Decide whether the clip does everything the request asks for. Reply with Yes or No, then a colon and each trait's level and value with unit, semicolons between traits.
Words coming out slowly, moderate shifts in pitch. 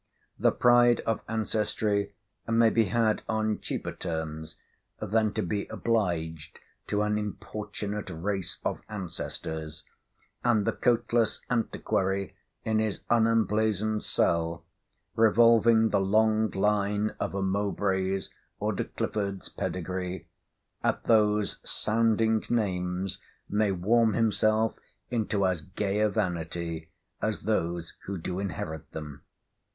Yes: slow, 115 wpm; average, 3.1 semitones